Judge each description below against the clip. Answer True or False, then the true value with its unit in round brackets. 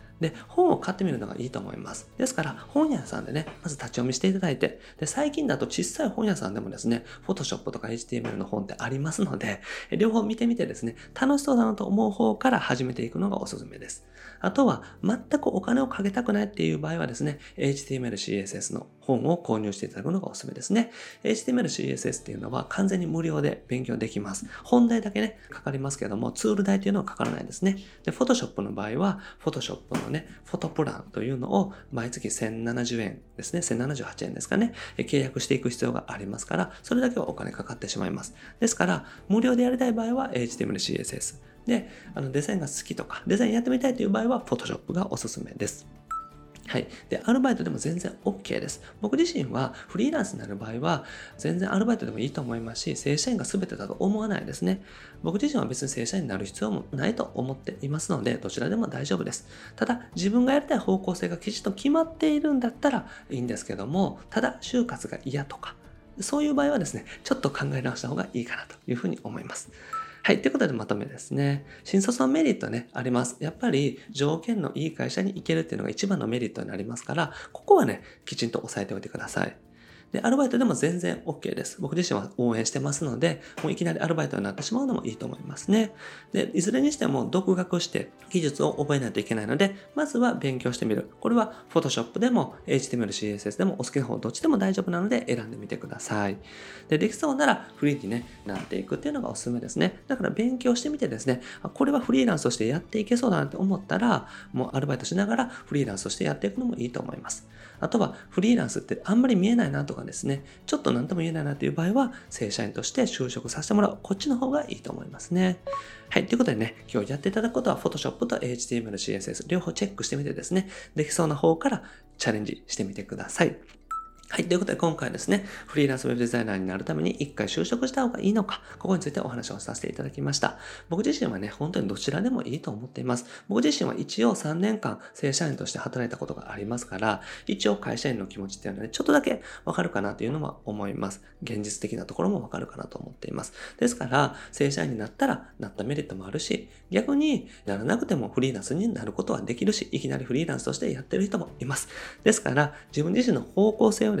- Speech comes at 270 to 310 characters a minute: False (490 characters per minute)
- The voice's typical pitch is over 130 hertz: True (185 Hz)